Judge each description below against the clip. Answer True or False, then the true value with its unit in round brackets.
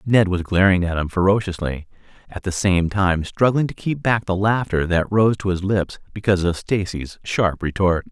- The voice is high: False (95 Hz)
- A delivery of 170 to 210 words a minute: True (190 wpm)